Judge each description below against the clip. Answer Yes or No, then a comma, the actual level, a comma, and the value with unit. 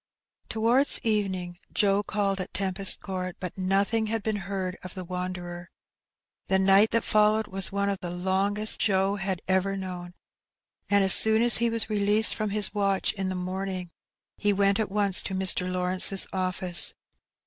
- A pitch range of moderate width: No, narrow, 2.1 semitones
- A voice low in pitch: No, high, 195 Hz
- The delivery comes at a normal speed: Yes, average, 170 wpm